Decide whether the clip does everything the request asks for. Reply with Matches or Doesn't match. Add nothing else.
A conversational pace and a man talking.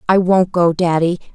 Doesn't match